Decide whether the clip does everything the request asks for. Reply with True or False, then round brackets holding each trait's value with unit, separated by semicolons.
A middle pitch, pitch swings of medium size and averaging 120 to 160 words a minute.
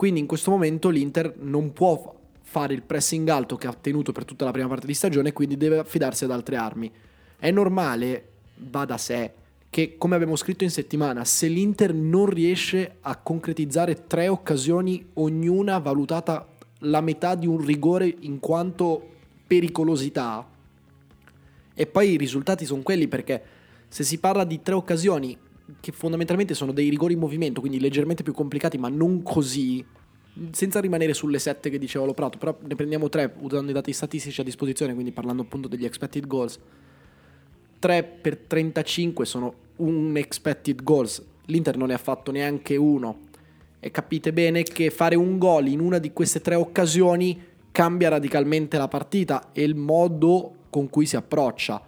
False (150 Hz; 3.9 semitones; 170 wpm)